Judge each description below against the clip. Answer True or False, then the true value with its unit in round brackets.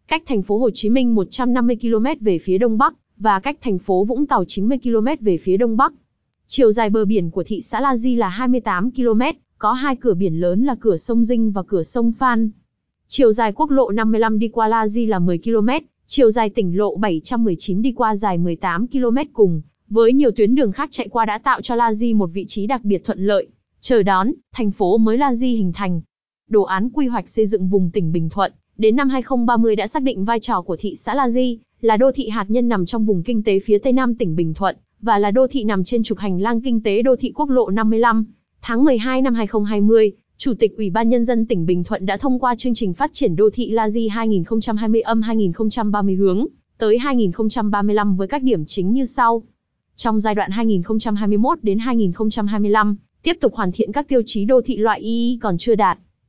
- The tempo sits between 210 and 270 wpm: True (225 wpm)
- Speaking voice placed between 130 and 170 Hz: False (225 Hz)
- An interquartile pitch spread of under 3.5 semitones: True (3.1 semitones)